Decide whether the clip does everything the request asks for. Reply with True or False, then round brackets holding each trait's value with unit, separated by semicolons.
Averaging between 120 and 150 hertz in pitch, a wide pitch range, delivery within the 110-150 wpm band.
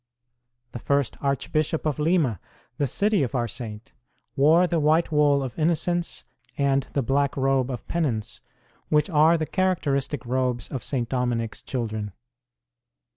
False (140 Hz; 4.0 semitones; 145 wpm)